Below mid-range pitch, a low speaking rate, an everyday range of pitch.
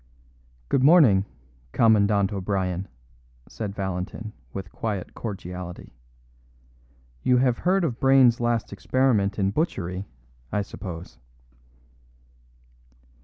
Yes: low, 100 Hz; slow, 90 wpm; average, 4.2 semitones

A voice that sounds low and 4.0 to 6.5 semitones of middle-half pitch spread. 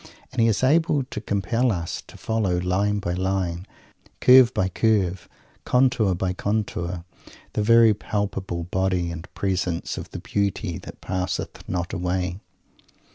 No: very low, 95 Hz; average, 3.5 semitones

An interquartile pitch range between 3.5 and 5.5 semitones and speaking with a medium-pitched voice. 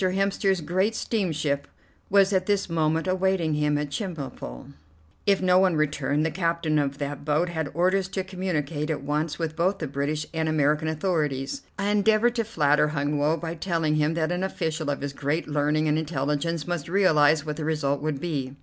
Yes: average, 3.8 semitones; medium, 160 Hz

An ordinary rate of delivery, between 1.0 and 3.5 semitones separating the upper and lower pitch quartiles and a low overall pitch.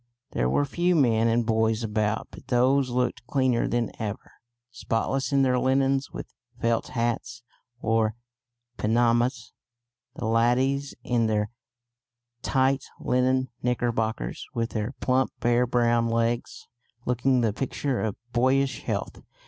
No: slow, 125 wpm; narrow, 2.5 semitones; low, 120 Hz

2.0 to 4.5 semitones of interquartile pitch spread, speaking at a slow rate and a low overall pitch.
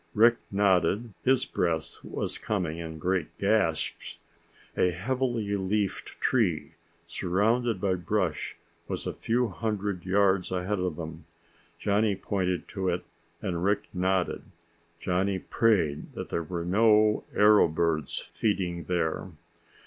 Yes: average, 3.3 semitones; slow, 125 wpm; very low, 95 Hz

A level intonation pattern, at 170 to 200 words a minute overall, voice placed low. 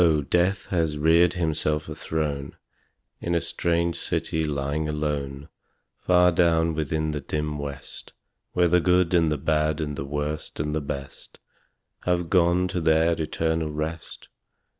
No: narrow, 2.2 semitones; average, 145 wpm; very low, 80 Hz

